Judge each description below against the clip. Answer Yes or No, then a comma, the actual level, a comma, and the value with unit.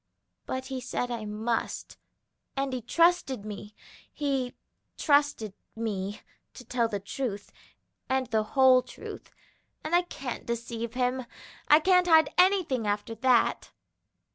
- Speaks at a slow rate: Yes, slow, 130 wpm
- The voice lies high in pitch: Yes, very high, 250 Hz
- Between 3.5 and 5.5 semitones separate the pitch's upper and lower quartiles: Yes, average, 3.8 semitones